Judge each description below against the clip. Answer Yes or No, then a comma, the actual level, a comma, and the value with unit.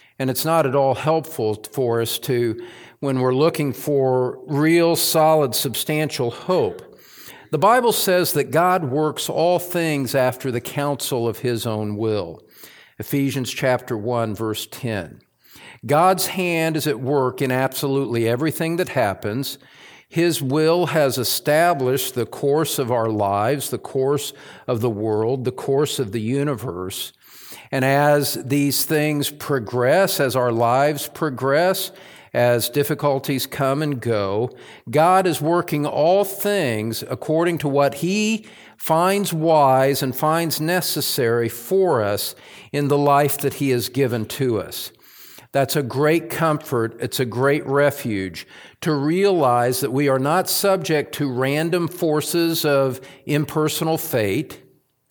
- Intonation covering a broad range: No, average, 4.0 semitones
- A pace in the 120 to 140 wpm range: Yes, slow, 135 wpm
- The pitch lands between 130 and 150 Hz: Yes, medium, 140 Hz